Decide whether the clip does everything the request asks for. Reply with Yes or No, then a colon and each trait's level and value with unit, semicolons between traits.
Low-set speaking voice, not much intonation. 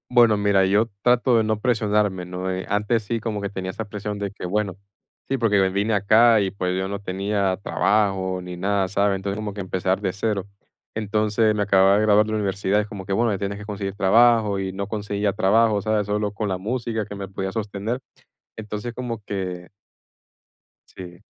Yes: low, 100 Hz; narrow, 2.0 semitones